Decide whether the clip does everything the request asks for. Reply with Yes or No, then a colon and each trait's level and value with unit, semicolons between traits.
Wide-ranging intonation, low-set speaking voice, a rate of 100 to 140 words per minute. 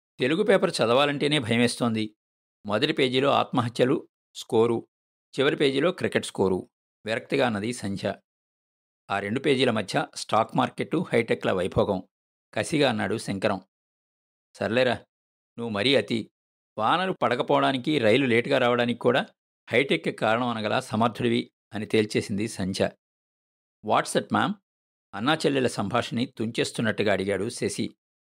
No: average, 3.9 semitones; low, 110 Hz; average, 105 wpm